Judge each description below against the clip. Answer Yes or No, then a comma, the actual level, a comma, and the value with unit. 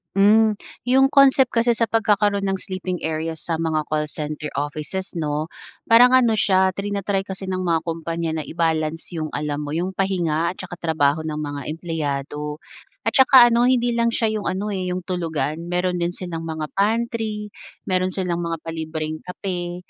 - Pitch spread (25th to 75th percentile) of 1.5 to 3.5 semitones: No, average, 4.5 semitones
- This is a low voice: No, medium, 180 Hz